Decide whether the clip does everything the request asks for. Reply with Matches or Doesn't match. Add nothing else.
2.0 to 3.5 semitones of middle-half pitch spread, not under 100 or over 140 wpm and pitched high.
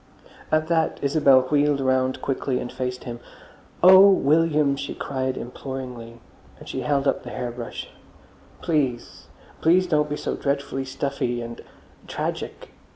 Doesn't match